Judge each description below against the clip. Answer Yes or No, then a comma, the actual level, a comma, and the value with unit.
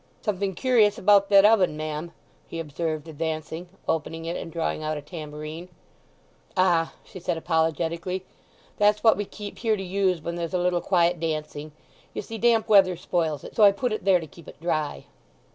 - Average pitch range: Yes, average, 3.6 semitones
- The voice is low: No, medium, 170 Hz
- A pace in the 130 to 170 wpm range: No, average, 185 wpm